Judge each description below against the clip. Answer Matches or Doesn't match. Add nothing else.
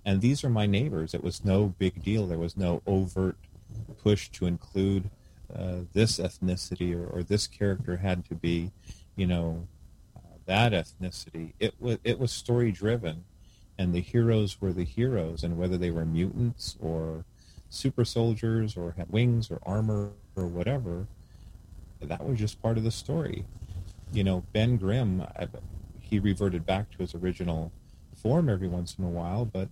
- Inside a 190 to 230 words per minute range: Doesn't match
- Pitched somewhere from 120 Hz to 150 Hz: Doesn't match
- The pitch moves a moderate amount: Matches